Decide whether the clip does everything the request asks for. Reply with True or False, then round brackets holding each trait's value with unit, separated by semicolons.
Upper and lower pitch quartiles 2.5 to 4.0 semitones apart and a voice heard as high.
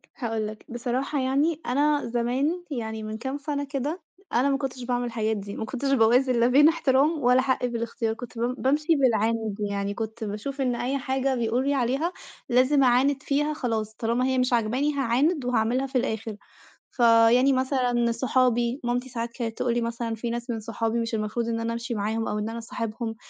True (2.9 semitones; 245 Hz)